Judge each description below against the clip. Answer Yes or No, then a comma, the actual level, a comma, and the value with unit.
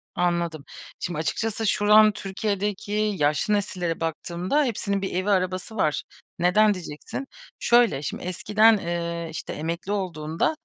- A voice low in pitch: No, medium, 185 Hz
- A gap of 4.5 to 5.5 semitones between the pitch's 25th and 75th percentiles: No, average, 3.7 semitones